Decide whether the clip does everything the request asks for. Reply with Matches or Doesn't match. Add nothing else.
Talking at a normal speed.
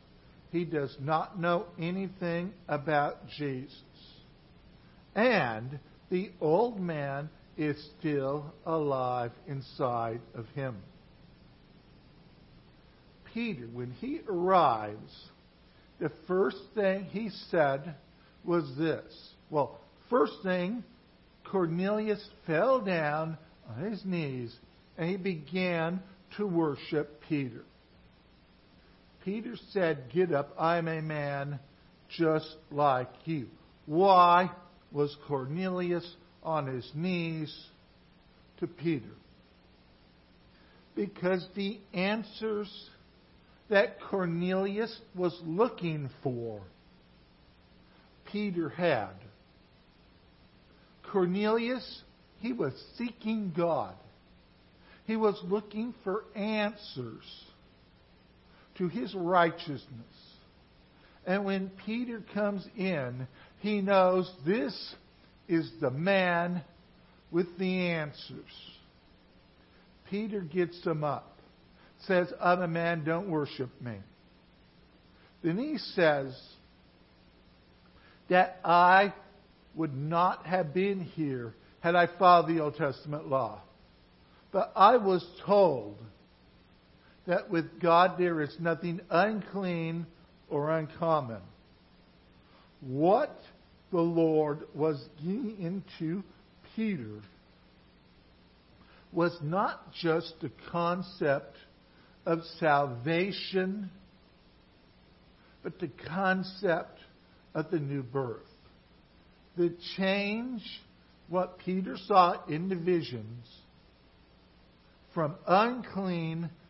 Doesn't match